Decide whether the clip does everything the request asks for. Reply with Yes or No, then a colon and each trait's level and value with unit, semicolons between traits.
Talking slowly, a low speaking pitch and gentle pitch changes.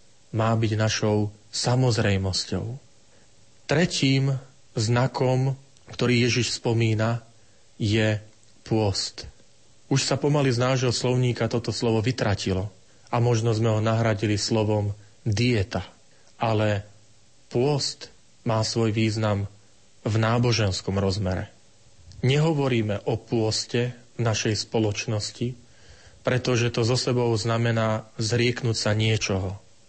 Yes: slow, 100 wpm; low, 115 Hz; narrow, 2.3 semitones